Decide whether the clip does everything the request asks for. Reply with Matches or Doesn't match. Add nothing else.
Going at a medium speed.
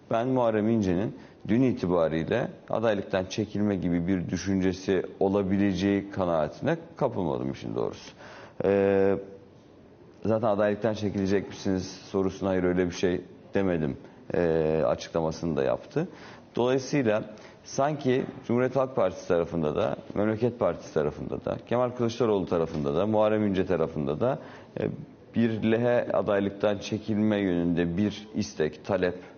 Matches